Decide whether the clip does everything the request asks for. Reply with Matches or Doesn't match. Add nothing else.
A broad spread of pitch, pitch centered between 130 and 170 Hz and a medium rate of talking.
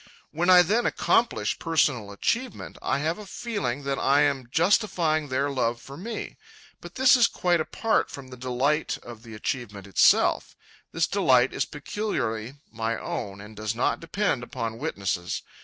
Matches